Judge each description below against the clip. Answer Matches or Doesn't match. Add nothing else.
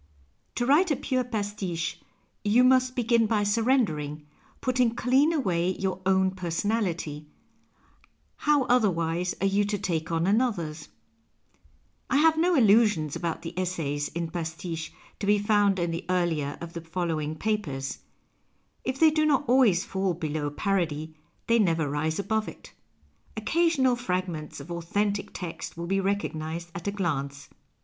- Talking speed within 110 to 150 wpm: Matches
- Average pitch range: Doesn't match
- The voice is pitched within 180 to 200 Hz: Matches